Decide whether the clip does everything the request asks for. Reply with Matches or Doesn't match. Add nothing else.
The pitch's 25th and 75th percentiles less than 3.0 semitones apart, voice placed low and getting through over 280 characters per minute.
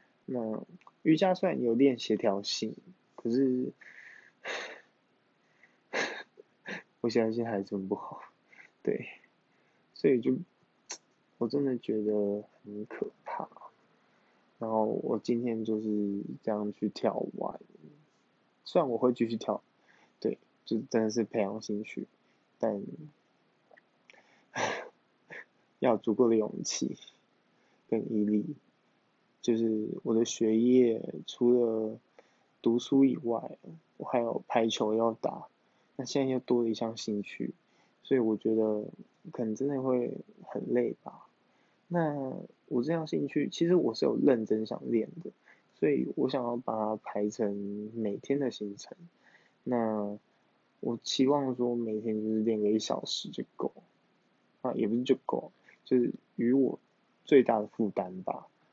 Doesn't match